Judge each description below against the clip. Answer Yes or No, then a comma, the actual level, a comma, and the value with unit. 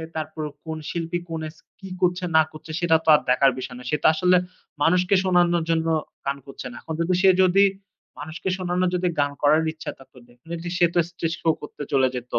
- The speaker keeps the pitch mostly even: No, average, 3.0 semitones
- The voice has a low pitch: No, medium, 165 Hz